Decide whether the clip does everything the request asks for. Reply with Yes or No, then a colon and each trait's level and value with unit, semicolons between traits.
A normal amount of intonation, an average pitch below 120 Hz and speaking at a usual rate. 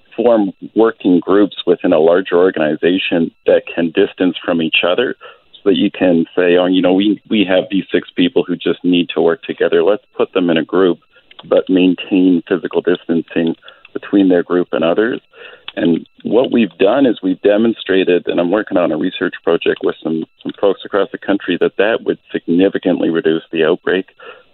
No: narrow, 2.0 semitones; very low, 90 Hz; average, 185 wpm